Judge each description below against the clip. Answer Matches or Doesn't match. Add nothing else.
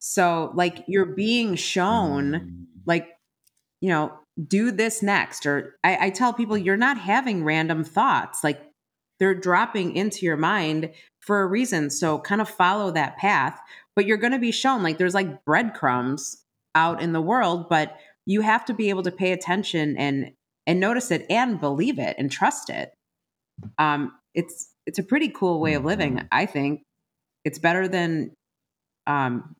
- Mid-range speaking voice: Matches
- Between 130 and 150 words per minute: Doesn't match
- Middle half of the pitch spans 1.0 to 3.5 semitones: Doesn't match